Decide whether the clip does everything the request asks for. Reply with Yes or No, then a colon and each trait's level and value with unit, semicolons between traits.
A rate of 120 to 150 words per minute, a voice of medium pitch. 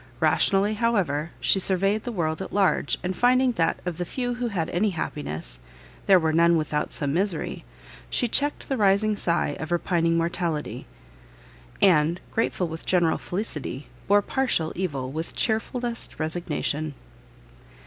Yes: average, 145 wpm; medium, 180 Hz